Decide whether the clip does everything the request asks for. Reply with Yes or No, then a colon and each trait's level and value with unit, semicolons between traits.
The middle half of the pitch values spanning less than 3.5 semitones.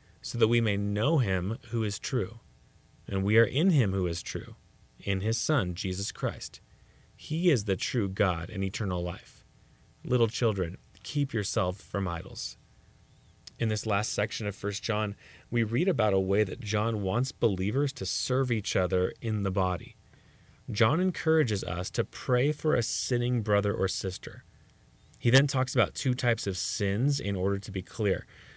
No: average, 4.1 semitones